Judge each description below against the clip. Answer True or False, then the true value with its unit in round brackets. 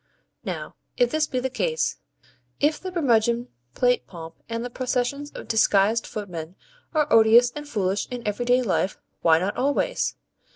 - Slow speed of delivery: False (155 wpm)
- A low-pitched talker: False (240 Hz)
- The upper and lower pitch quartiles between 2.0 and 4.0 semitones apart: False (5.1 semitones)